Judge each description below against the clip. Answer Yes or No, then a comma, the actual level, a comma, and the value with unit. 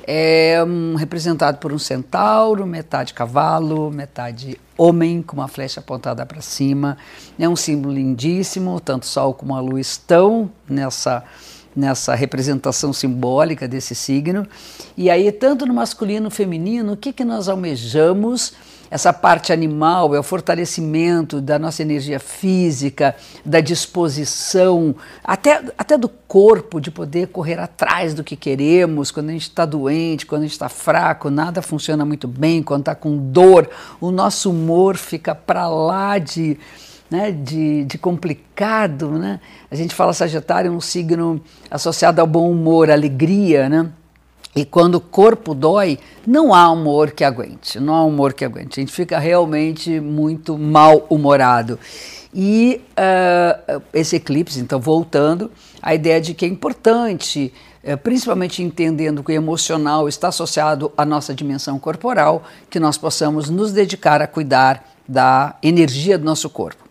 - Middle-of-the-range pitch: Yes, medium, 160 Hz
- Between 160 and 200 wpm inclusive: No, average, 150 wpm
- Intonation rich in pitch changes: No, average, 3.3 semitones